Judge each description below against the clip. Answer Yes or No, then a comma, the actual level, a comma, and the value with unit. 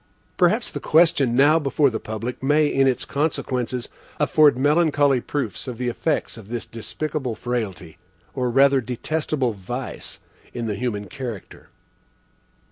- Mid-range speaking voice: No, low, 130 Hz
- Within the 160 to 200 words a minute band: No, slow, 135 wpm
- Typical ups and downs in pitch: Yes, average, 3.9 semitones